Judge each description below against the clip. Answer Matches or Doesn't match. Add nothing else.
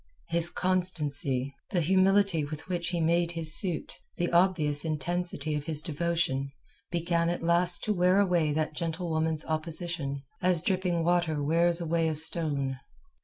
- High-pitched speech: Doesn't match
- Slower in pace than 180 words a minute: Matches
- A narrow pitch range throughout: Matches